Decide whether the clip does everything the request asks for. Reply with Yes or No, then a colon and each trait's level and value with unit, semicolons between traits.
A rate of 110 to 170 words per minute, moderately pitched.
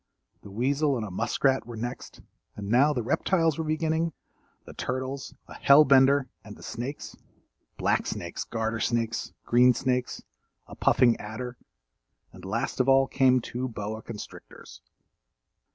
No: slow, 135 wpm; low, 125 Hz